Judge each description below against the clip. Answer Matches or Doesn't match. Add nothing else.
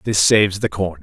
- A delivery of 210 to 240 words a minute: Matches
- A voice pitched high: Doesn't match